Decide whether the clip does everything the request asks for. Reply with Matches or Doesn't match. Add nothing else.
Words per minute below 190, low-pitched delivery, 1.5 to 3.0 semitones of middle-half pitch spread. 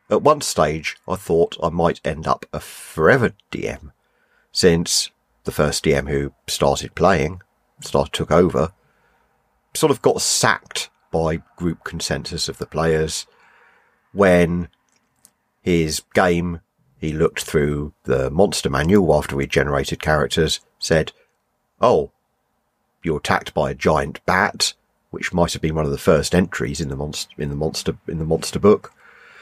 Matches